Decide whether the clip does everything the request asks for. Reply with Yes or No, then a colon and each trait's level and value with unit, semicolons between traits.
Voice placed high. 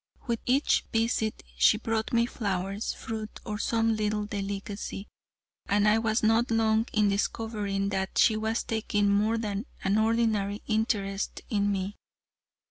Yes: high, 215 Hz